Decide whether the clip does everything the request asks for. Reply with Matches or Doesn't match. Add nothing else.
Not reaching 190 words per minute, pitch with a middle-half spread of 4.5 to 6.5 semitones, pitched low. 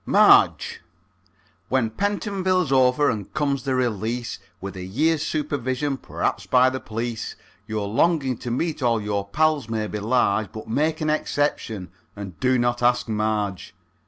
Matches